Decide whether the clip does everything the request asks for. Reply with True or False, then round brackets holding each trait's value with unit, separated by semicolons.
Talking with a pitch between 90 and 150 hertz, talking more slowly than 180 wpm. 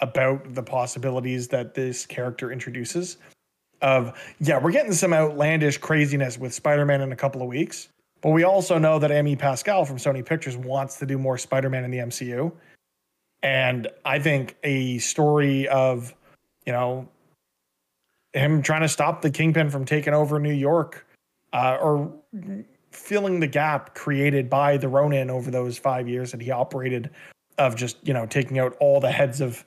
True (140 Hz; 170 wpm)